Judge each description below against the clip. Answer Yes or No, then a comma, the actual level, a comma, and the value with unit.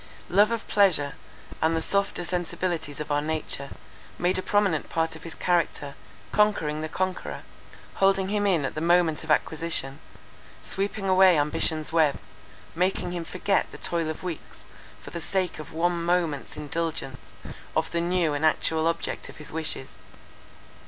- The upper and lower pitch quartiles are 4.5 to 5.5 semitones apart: No, average, 2.9 semitones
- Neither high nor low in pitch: Yes, medium, 165 Hz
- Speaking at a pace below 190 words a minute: Yes, average, 160 wpm